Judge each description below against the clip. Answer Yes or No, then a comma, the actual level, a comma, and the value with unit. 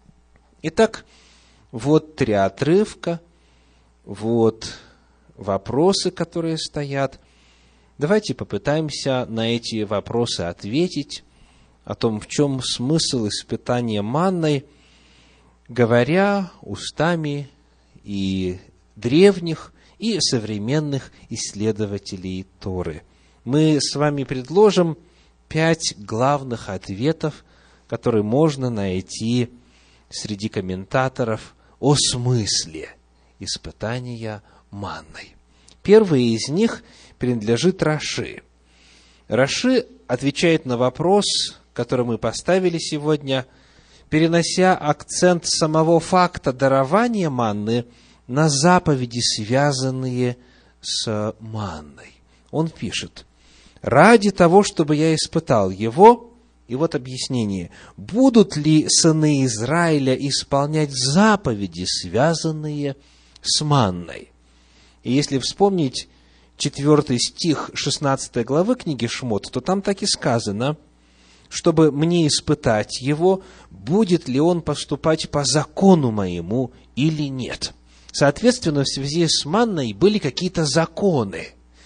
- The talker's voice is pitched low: Yes, low, 130 Hz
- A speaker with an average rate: No, slow, 90 wpm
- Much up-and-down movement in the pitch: Yes, wide, 8.4 semitones